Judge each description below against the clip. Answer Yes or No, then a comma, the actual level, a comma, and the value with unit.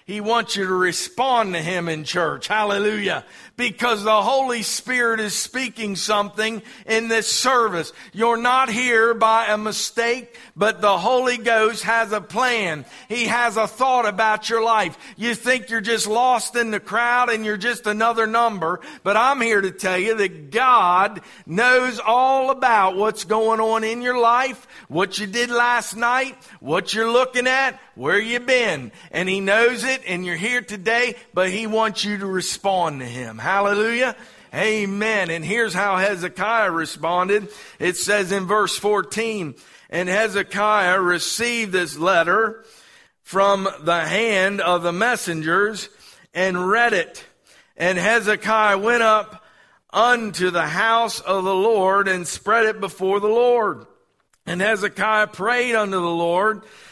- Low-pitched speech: No, high, 215 Hz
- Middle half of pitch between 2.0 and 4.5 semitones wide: Yes, average, 3.3 semitones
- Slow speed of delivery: No, average, 155 wpm